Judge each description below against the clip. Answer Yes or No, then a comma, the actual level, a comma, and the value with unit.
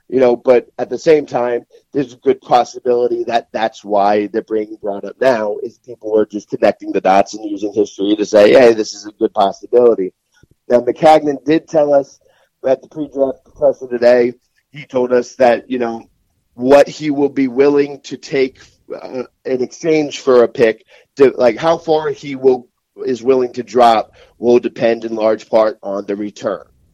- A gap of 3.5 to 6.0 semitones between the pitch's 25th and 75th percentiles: Yes, average, 4.4 semitones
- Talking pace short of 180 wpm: No, average, 185 wpm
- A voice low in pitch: Yes, low, 125 Hz